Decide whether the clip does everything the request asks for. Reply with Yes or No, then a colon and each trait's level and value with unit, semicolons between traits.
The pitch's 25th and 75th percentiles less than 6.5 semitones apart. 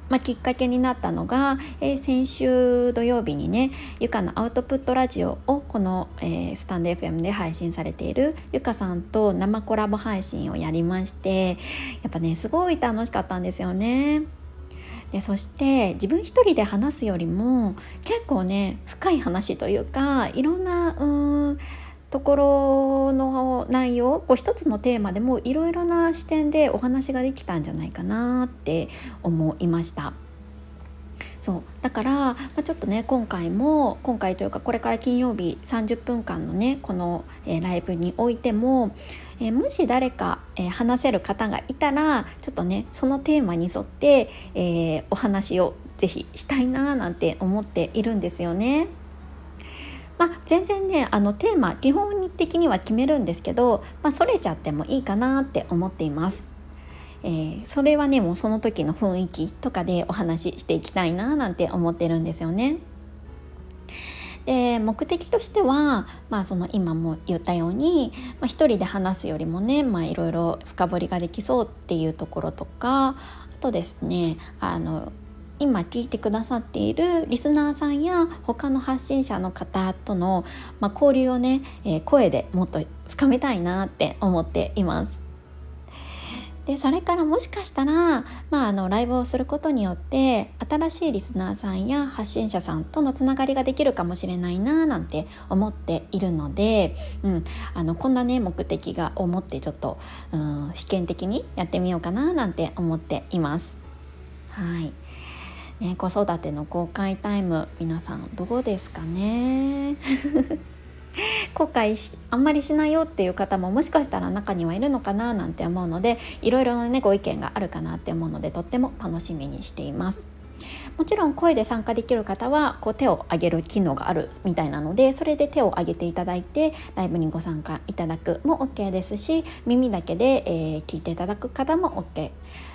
No: wide, 7.7 semitones